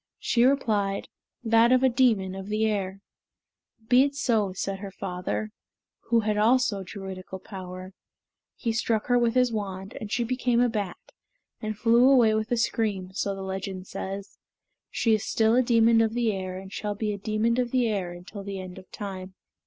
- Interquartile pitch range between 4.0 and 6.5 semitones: No, average, 3.3 semitones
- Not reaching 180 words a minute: No, average, 190 wpm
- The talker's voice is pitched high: Yes, high, 215 Hz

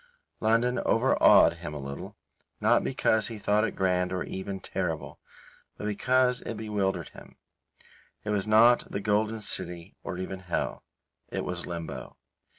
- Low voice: Yes, low, 100 Hz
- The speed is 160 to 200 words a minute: No, average, 150 wpm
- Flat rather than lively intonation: No, average, 3.3 semitones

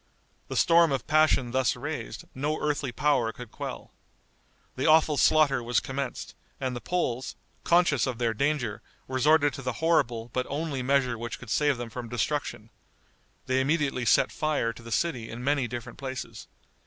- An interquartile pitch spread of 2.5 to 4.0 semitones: Yes, average, 3.5 semitones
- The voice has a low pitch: Yes, low, 130 Hz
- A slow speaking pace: No, average, 165 wpm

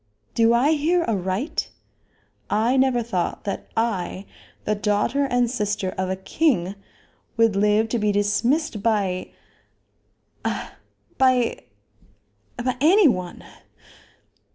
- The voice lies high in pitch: Yes, high, 225 Hz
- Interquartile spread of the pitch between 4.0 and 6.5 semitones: Yes, average, 4.3 semitones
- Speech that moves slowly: Yes, slow, 110 wpm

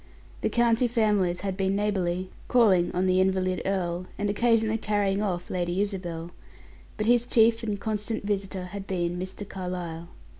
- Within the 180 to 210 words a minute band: No, average, 155 wpm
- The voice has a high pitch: Yes, high, 195 Hz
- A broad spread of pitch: No, average, 2.8 semitones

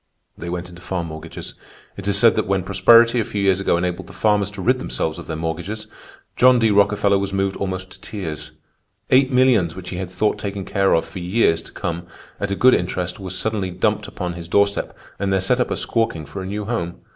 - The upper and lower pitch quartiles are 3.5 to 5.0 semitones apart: No, average, 2.9 semitones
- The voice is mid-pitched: No, very low, 95 Hz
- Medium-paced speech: No, fast, 225 wpm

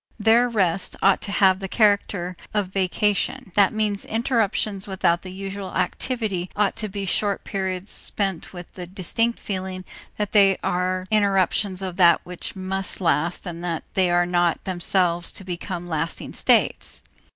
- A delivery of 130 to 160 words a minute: Yes, average, 155 wpm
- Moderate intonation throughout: No, narrow, 2.2 semitones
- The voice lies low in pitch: No, high, 190 Hz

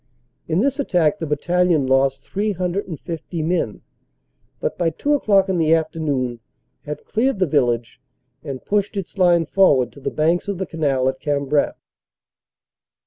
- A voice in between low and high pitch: Yes, medium, 165 Hz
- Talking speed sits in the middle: Yes, average, 155 wpm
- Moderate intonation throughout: Yes, average, 5.0 semitones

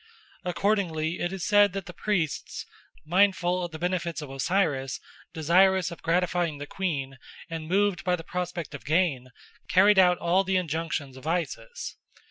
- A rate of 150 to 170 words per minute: Yes, average, 155 wpm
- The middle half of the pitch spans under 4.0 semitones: Yes, average, 2.9 semitones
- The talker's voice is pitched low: No, medium, 175 Hz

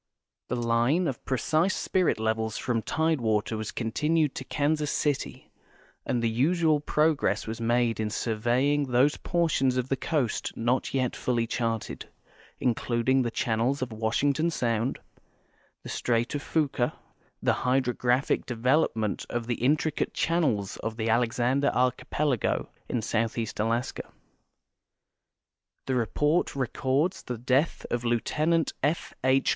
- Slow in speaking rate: Yes, slow, 130 wpm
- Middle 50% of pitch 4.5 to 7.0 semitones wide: No, average, 3.9 semitones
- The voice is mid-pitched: No, low, 125 Hz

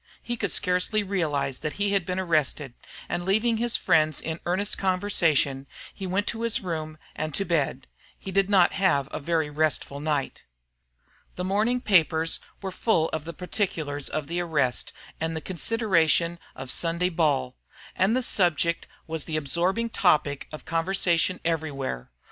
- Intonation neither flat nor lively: Yes, average, 3.9 semitones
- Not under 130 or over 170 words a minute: Yes, average, 160 wpm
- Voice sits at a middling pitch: Yes, medium, 170 Hz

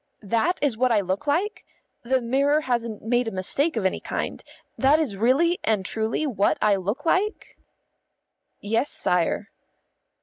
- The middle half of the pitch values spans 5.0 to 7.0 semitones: Yes, wide, 5.5 semitones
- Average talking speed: Yes, average, 155 wpm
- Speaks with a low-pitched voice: No, high, 240 Hz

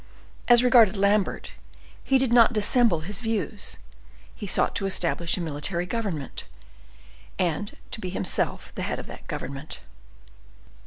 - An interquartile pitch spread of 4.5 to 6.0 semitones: Yes, average, 4.9 semitones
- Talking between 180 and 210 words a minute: No, average, 140 wpm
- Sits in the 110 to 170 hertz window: No, high, 200 Hz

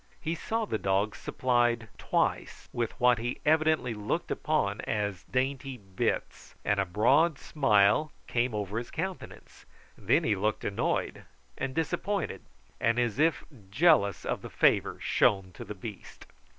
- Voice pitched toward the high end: No, low, 120 Hz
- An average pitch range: No, wide, 5.9 semitones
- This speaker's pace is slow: No, average, 145 wpm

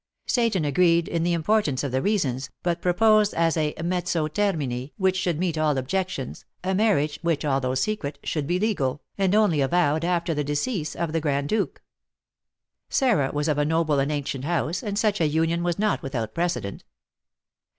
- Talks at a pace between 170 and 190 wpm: Yes, average, 180 wpm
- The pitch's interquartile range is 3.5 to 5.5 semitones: Yes, average, 4.3 semitones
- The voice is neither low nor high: Yes, medium, 165 Hz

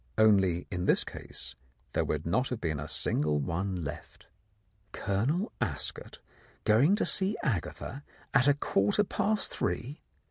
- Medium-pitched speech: No, low, 105 Hz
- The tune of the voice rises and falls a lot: Yes, wide, 8.9 semitones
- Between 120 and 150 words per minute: Yes, average, 140 wpm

